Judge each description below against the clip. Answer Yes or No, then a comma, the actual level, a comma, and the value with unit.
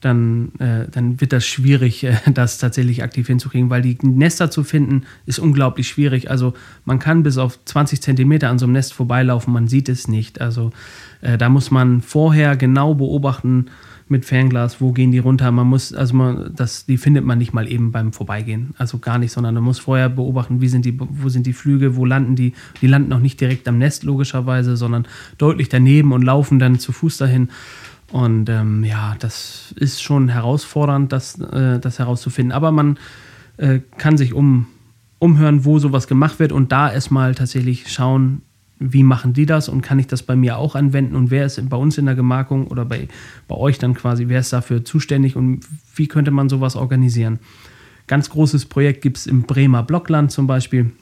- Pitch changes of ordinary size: No, narrow, 2.0 semitones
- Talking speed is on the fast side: Yes, fast, 200 wpm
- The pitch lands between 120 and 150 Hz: Yes, low, 130 Hz